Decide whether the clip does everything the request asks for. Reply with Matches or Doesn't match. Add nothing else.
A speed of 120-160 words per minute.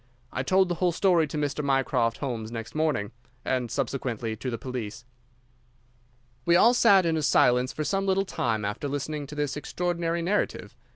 Doesn't match